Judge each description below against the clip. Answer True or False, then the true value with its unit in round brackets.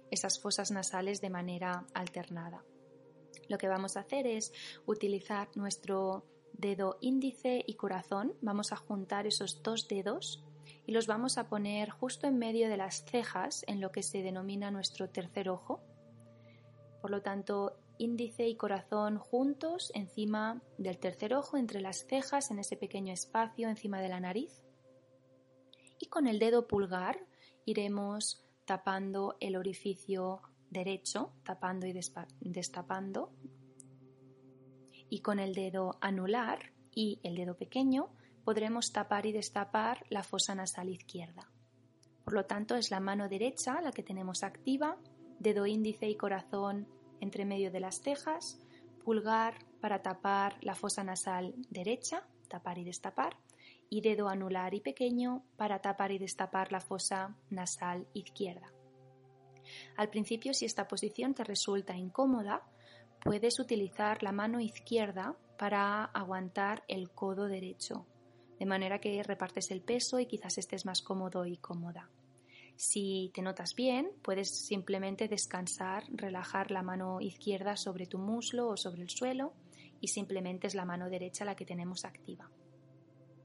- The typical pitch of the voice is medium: False (195 Hz)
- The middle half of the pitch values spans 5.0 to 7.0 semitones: False (2.8 semitones)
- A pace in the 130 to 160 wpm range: True (140 wpm)